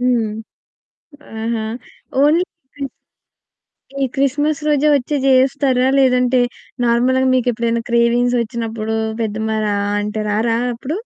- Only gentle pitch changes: No, average, 3.0 semitones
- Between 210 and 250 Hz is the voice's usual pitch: Yes, high, 245 Hz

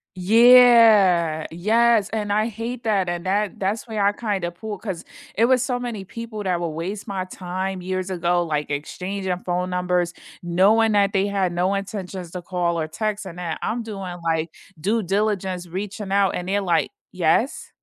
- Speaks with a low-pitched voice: No, high, 190 Hz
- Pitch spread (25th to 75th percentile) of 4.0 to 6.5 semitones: No, average, 3.2 semitones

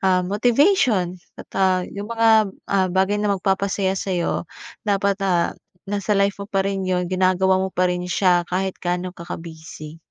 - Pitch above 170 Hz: Yes, high, 190 Hz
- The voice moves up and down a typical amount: No, narrow, 1.9 semitones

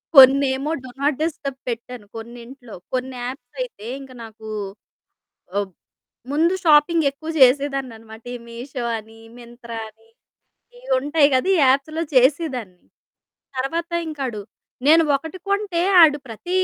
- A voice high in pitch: Yes, very high, 265 Hz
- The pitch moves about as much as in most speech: Yes, average, 4.4 semitones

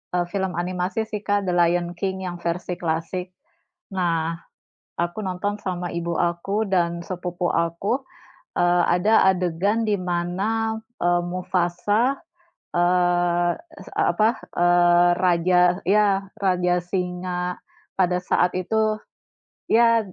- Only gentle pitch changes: Yes, narrow, 2.0 semitones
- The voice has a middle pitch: Yes, medium, 180 Hz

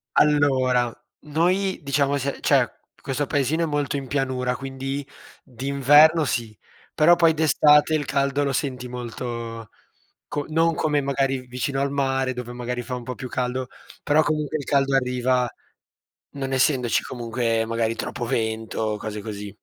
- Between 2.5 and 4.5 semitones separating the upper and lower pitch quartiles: Yes, average, 2.8 semitones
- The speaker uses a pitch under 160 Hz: Yes, low, 135 Hz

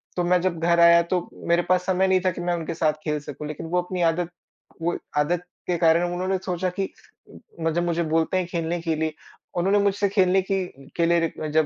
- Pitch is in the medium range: Yes, medium, 175 Hz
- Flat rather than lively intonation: Yes, narrow, 1.8 semitones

